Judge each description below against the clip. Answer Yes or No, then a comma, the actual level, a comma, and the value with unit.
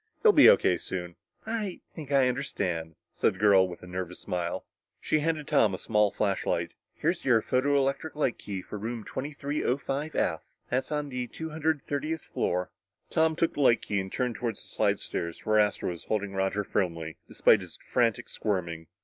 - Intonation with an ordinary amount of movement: No, wide, 7.3 semitones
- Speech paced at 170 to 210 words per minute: Yes, average, 180 wpm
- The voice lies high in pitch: No, low, 115 Hz